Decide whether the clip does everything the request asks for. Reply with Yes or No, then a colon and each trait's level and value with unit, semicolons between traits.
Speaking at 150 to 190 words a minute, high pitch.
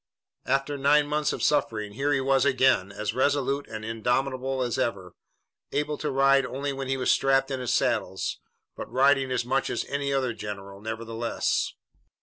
No: average, 170 wpm; low, 135 Hz